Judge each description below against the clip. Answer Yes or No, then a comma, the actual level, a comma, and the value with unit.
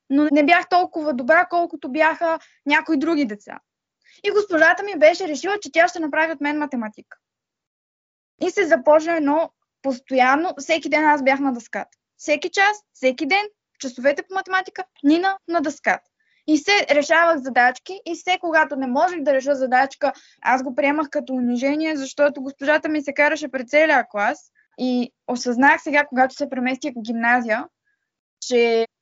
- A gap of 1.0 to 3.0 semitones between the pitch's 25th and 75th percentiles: No, average, 3.8 semitones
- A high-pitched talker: Yes, very high, 300 Hz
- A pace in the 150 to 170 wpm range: Yes, average, 160 wpm